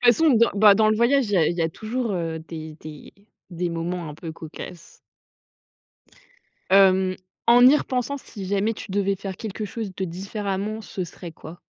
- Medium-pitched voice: No, high, 195 Hz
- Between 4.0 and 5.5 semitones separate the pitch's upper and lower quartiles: Yes, average, 4.3 semitones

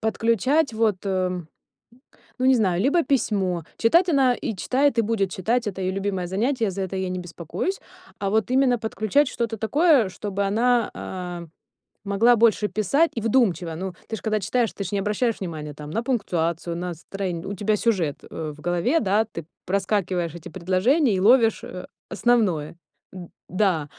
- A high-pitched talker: Yes, high, 200 Hz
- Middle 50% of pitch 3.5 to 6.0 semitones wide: Yes, average, 4.4 semitones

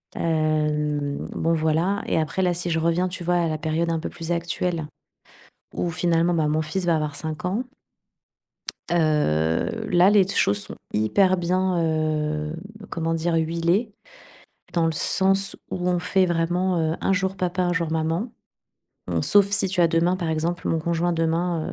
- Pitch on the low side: No, medium, 170 Hz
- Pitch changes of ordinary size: No, narrow, 2.3 semitones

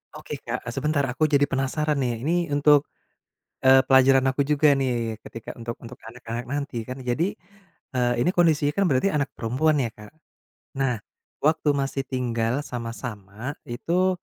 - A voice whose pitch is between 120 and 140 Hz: Yes, low, 135 Hz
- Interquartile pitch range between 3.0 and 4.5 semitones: Yes, average, 3.6 semitones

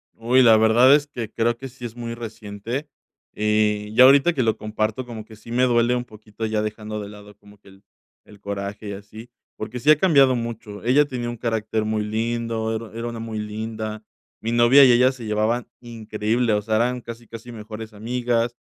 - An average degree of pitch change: No, narrow, 2.1 semitones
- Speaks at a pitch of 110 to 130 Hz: Yes, low, 115 Hz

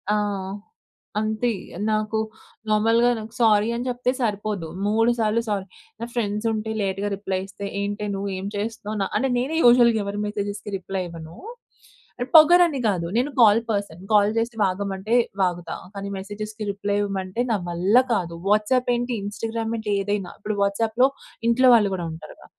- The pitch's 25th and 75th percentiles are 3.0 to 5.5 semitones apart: No, narrow, 2.4 semitones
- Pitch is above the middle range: Yes, high, 210 Hz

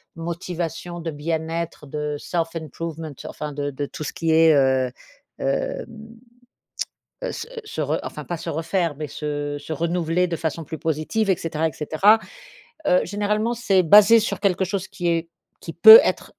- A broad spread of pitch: No, average, 2.9 semitones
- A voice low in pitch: No, medium, 165 Hz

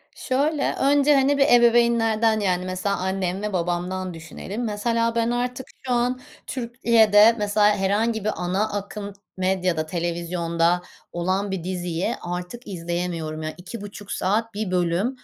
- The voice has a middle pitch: No, high, 200 Hz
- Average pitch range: Yes, average, 4.6 semitones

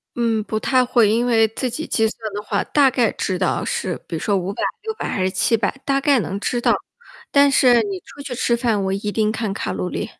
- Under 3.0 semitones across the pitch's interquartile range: No, average, 3.7 semitones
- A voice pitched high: Yes, high, 225 Hz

